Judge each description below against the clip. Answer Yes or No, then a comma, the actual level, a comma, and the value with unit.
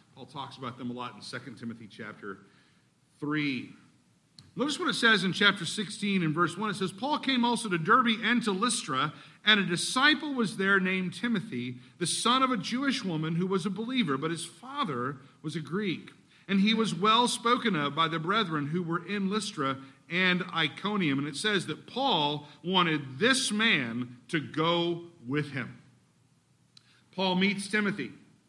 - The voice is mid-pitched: Yes, medium, 180 Hz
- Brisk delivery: No, average, 175 wpm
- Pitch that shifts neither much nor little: No, wide, 6.3 semitones